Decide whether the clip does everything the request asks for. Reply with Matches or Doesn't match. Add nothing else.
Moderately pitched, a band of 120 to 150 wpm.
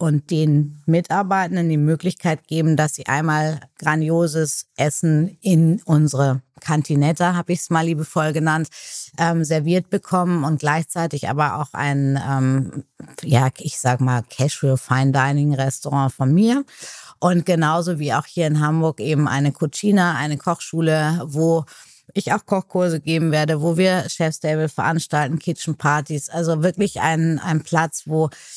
Matches